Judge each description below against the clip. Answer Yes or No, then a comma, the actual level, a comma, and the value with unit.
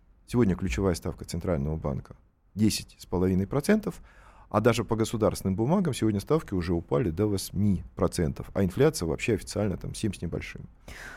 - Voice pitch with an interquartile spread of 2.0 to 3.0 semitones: No, average, 3.7 semitones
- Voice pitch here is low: Yes, low, 100 Hz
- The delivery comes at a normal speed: Yes, average, 135 wpm